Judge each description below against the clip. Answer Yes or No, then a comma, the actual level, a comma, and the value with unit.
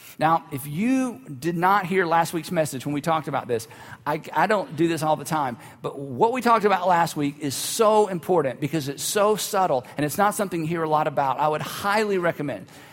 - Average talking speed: No, fast, 230 wpm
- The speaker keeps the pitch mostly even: No, average, 4.7 semitones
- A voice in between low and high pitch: Yes, medium, 160 Hz